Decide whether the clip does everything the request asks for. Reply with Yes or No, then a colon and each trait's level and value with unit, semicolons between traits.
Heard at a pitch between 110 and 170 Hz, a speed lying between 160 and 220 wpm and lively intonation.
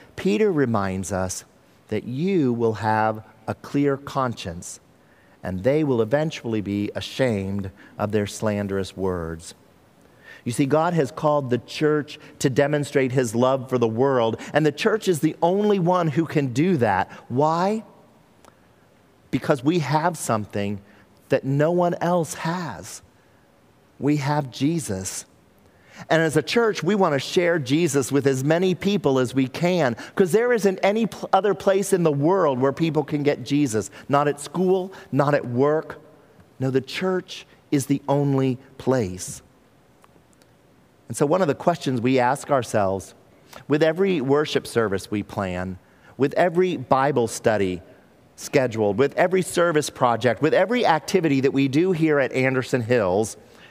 No: medium, 140 Hz; average, 150 wpm; wide, 5.9 semitones